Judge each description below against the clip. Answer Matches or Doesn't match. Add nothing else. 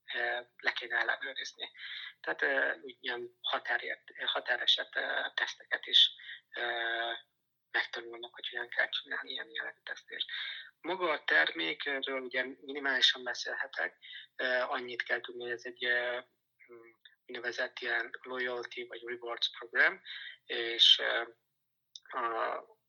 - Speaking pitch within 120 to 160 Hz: Matches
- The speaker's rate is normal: Doesn't match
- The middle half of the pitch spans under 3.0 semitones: Matches